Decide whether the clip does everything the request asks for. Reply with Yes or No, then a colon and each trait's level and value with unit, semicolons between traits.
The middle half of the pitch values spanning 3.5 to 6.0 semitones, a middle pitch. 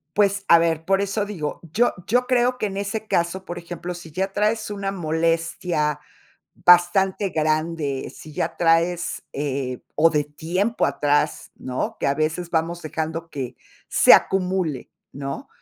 Yes: average, 3.9 semitones; medium, 170 Hz